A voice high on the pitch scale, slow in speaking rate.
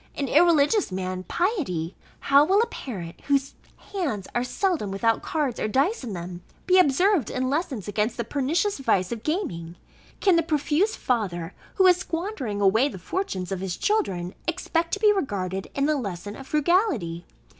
No: very high, 270 Hz; average, 170 wpm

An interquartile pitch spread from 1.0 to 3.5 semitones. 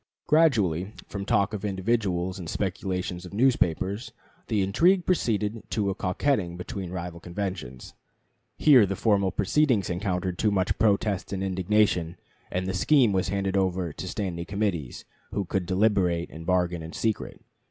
Yes: average, 2.8 semitones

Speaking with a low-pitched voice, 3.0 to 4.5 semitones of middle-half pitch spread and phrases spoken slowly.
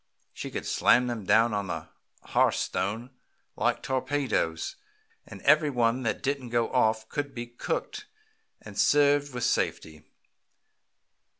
Yes: low, 120 Hz; average, 4.1 semitones; slow, 130 wpm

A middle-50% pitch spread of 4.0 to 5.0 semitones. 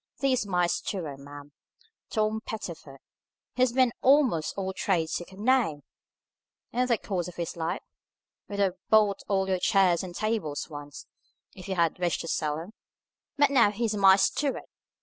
Yes: average, 4.5 semitones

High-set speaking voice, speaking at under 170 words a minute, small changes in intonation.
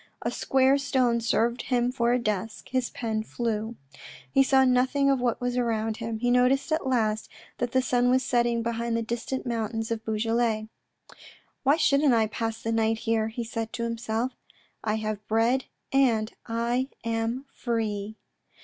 No: high, 235 Hz; average, 175 wpm; narrow, 2.1 semitones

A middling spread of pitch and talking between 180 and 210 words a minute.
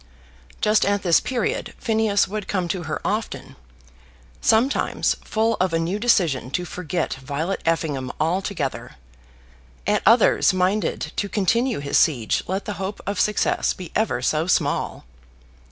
No: average, 4.5 semitones; average, 140 wpm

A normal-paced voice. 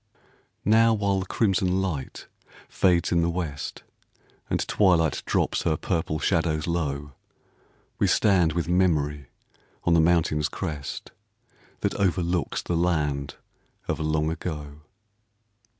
No: slow, 120 wpm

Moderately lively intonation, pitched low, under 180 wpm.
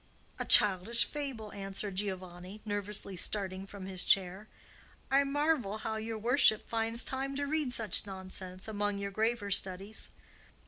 No: average, 3.3 semitones; high, 205 Hz; average, 140 wpm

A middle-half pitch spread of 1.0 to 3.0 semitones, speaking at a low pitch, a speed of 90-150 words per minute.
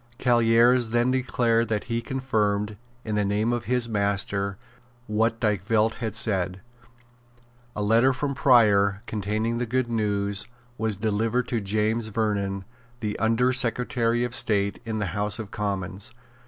Yes: narrow, 2.6 semitones; low, 110 Hz; average, 140 wpm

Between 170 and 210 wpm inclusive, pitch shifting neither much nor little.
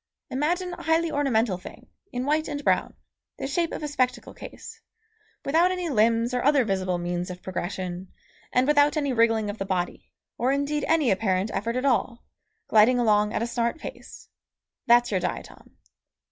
No: average, 175 wpm; wide, 5.8 semitones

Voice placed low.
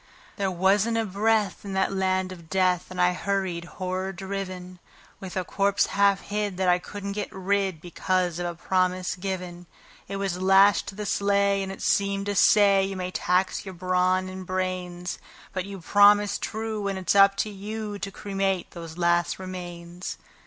No: high, 190 Hz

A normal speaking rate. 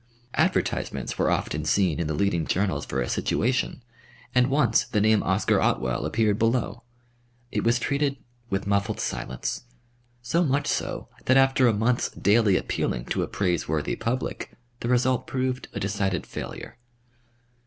Yes: average, 150 wpm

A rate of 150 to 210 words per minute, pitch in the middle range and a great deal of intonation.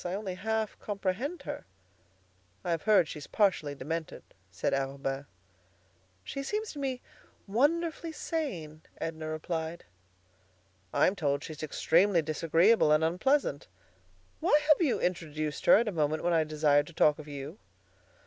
No: average, 140 wpm; medium, 170 Hz; wide, 6.1 semitones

